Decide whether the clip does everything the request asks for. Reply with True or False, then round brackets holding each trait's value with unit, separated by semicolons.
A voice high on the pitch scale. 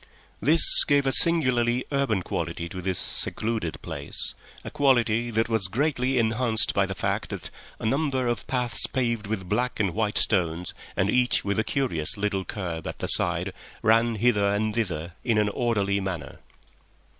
False (110 Hz)